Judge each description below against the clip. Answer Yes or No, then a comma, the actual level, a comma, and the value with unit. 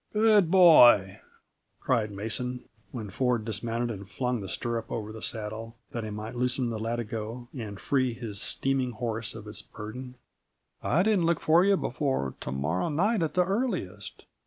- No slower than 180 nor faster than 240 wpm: No, average, 170 wpm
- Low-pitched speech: Yes, low, 120 Hz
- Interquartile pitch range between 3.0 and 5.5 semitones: Yes, average, 4.0 semitones